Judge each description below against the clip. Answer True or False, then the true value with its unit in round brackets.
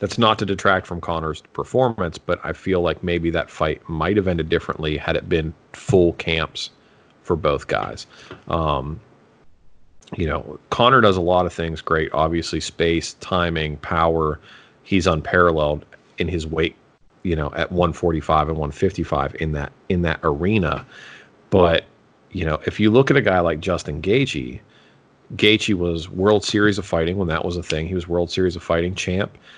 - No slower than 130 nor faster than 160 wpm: False (175 wpm)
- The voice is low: True (85 Hz)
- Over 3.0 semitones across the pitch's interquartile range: False (2.6 semitones)